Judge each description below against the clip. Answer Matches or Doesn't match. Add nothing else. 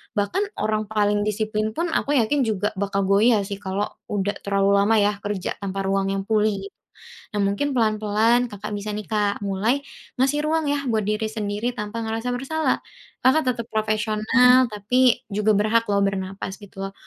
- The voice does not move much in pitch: Matches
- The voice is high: Matches